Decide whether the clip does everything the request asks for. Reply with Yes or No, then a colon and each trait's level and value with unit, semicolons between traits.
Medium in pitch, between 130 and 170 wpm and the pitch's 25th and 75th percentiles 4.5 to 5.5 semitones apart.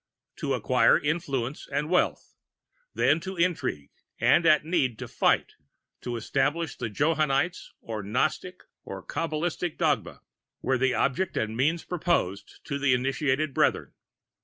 Yes: medium, 145 Hz; slow, 135 wpm; average, 4.8 semitones